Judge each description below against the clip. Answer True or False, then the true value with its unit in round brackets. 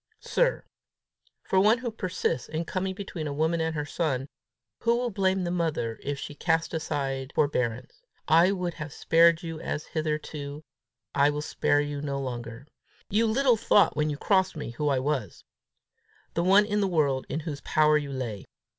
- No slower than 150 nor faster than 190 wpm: True (180 wpm)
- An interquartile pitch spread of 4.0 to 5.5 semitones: True (4.7 semitones)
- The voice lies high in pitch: False (155 Hz)